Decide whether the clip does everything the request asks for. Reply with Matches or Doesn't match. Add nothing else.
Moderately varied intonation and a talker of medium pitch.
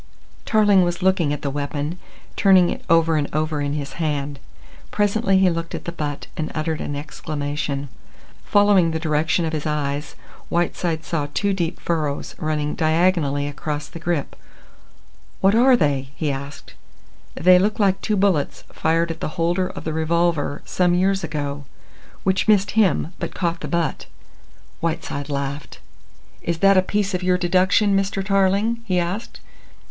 Matches